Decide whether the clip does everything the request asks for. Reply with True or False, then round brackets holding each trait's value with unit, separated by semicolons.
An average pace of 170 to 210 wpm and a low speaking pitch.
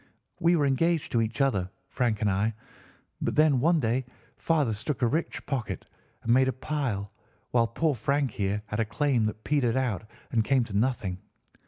True (185 wpm; 120 Hz)